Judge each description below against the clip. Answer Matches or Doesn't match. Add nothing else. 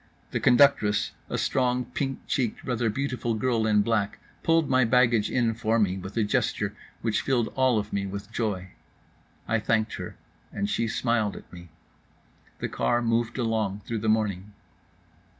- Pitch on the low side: Matches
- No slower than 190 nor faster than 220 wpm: Doesn't match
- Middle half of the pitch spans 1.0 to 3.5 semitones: Matches